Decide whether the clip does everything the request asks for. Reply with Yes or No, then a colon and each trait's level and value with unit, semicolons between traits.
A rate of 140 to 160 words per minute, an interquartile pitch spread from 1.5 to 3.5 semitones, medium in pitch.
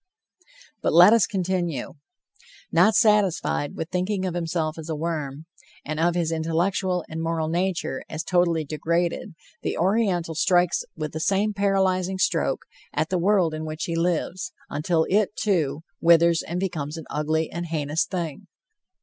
Yes: average, 155 wpm; average, 2.7 semitones; medium, 170 Hz